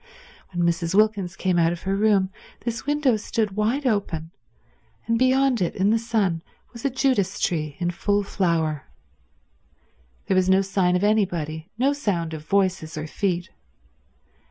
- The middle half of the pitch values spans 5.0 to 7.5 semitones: No, average, 4.2 semitones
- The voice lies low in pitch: No, high, 195 Hz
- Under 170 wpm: Yes, average, 155 wpm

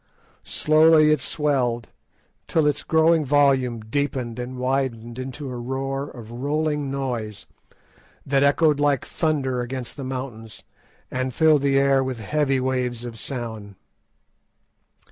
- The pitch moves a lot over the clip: No, average, 2.9 semitones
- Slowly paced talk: Yes, slow, 125 wpm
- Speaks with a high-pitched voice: No, low, 135 Hz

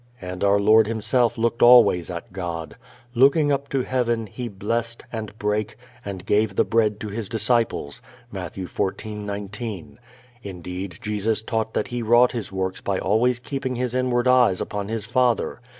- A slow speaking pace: No, average, 160 wpm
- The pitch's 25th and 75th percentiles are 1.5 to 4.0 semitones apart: Yes, average, 3.2 semitones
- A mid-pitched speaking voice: No, low, 110 Hz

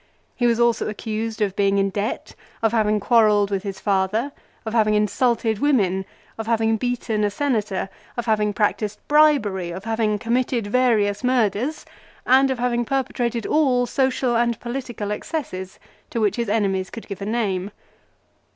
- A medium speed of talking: Yes, average, 160 wpm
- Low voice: No, high, 220 Hz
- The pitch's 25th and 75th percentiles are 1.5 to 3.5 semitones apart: Yes, average, 3.0 semitones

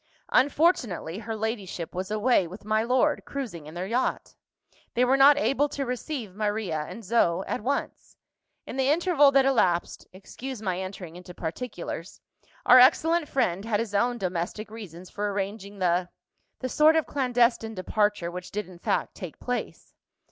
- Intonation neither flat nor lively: No, wide, 5.7 semitones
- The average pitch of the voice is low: No, high, 215 Hz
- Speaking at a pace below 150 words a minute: No, average, 160 wpm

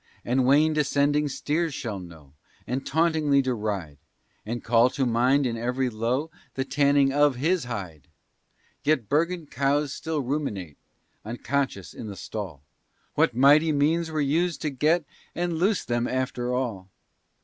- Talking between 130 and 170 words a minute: Yes, average, 145 wpm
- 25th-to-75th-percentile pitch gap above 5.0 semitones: No, average, 4.2 semitones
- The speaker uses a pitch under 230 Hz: Yes, low, 135 Hz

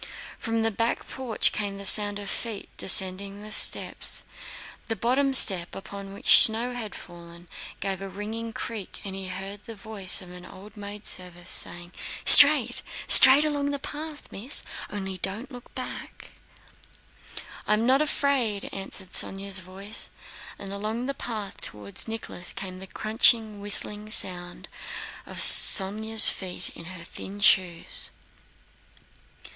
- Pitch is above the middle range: Yes, high, 205 Hz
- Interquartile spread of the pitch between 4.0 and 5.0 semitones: No, average, 2.9 semitones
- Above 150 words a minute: No, average, 140 wpm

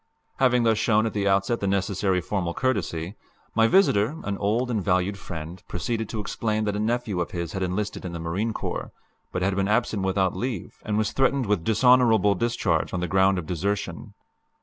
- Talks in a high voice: No, low, 100 Hz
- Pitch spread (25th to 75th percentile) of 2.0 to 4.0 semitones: Yes, average, 3.5 semitones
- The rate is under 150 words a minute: No, average, 195 wpm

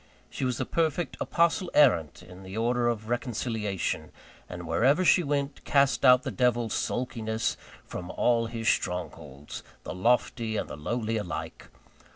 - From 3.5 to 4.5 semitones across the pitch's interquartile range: Yes, average, 4.0 semitones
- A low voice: Yes, low, 115 Hz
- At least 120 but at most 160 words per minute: Yes, average, 150 wpm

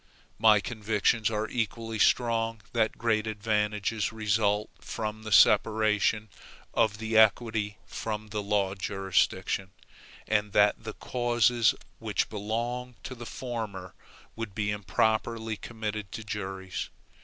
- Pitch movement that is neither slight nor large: No, narrow, 1.5 semitones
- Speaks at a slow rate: Yes, slow, 120 wpm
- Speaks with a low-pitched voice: Yes, low, 110 Hz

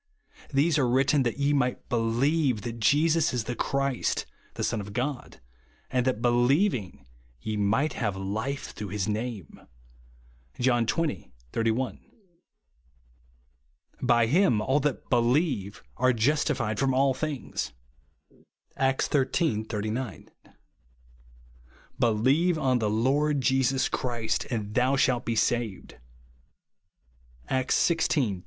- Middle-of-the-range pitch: No, low, 125 Hz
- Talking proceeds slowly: Yes, slow, 120 wpm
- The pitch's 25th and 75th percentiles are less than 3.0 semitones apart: No, average, 4.2 semitones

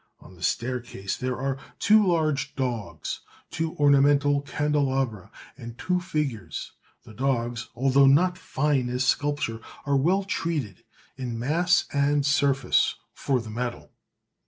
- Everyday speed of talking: No, slow, 130 wpm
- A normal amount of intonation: Yes, average, 3.3 semitones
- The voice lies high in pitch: No, low, 135 Hz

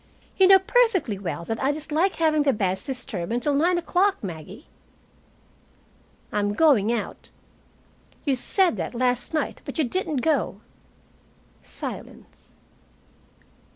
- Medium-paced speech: No, slow, 120 wpm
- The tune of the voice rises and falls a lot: Yes, wide, 7.2 semitones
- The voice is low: No, very high, 280 Hz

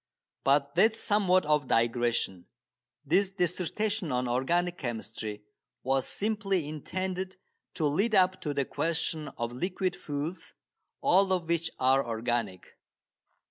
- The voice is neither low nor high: Yes, medium, 160 Hz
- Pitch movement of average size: No, wide, 6.5 semitones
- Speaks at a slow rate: Yes, slow, 130 wpm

